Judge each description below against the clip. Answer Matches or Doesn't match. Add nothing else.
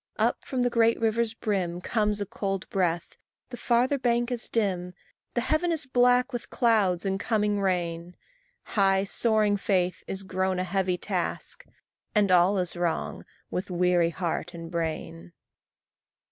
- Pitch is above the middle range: Matches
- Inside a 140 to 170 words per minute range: Matches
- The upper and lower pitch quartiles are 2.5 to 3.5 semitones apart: Doesn't match